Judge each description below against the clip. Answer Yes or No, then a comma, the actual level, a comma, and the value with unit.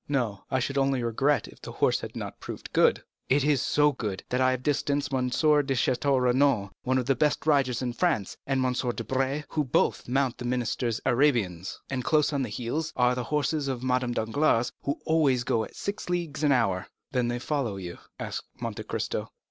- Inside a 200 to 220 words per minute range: Yes, fast, 205 wpm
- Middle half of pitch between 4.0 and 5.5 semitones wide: No, average, 2.8 semitones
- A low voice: Yes, low, 130 Hz